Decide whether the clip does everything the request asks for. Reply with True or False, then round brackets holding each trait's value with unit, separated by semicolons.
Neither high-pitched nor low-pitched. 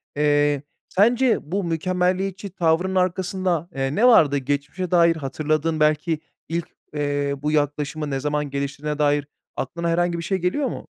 True (160 Hz)